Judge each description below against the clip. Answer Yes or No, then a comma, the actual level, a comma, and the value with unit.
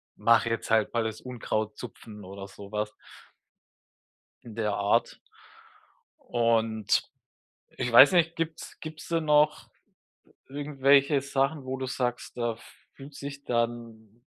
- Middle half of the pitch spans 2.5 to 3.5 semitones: No, average, 4.0 semitones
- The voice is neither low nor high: No, low, 120 Hz